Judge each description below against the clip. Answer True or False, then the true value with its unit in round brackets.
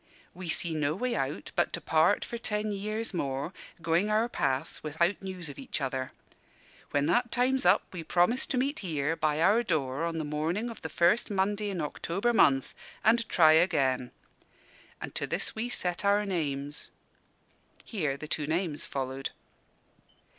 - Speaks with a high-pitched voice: False (170 Hz)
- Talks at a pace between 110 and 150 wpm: False (170 wpm)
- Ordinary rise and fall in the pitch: False (5.9 semitones)